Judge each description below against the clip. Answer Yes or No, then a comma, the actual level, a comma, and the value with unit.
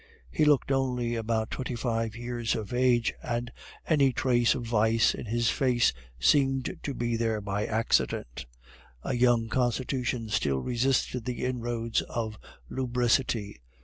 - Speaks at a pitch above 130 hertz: No, low, 120 Hz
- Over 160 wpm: No, average, 140 wpm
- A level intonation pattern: Yes, narrow, 1.9 semitones